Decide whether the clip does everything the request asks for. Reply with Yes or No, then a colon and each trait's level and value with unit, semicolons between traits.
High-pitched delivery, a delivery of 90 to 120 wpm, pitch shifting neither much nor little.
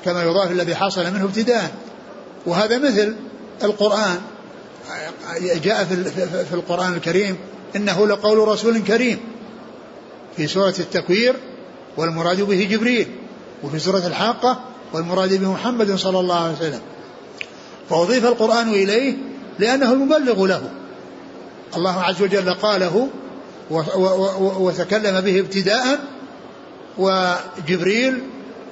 Yes: high, 195 Hz; average, 100 wpm; average, 3.9 semitones